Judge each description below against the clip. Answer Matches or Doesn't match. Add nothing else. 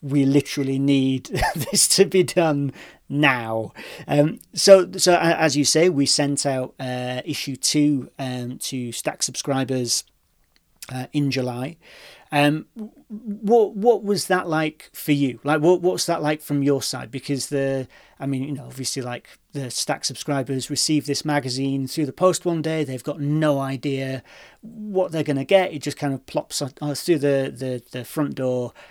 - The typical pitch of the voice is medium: Matches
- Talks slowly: Doesn't match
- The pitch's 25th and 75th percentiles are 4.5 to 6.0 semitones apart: Doesn't match